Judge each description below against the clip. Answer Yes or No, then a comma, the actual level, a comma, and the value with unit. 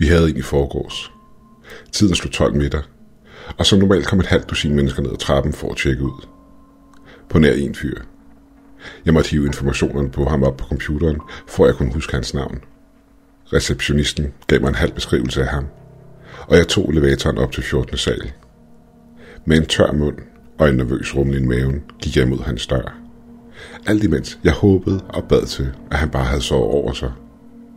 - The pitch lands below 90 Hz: Yes, very low, 75 Hz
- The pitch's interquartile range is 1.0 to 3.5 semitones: Yes, average, 3.1 semitones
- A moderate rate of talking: Yes, average, 190 wpm